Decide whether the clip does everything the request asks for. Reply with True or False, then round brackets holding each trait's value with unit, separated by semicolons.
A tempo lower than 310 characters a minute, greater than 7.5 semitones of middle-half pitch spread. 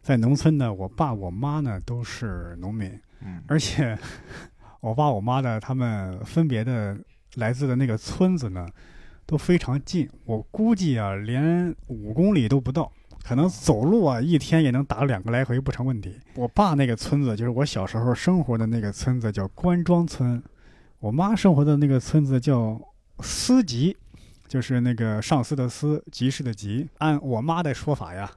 False (255 characters per minute; 5.3 semitones)